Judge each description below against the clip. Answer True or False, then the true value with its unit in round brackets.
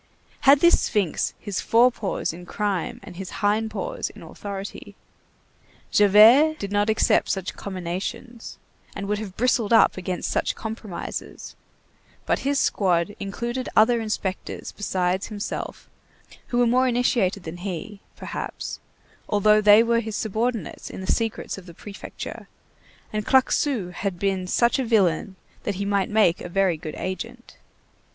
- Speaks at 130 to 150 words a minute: True (145 wpm)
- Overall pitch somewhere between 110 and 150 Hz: False (205 Hz)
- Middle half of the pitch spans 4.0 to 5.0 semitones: False (3.5 semitones)